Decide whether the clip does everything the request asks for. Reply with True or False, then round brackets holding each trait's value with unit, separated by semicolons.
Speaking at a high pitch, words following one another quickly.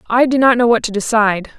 True (230 Hz; 265 wpm)